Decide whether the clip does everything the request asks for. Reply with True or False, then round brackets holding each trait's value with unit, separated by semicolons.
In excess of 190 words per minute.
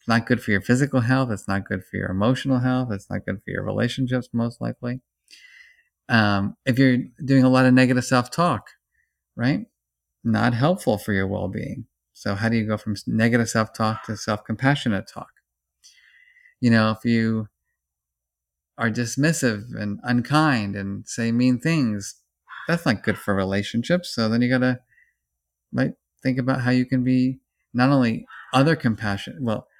False (165 wpm)